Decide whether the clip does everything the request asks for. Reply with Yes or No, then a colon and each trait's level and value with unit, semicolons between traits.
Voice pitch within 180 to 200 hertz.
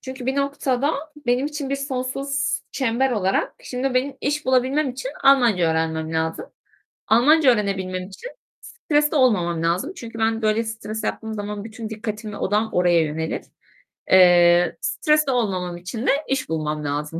No: high, 225 Hz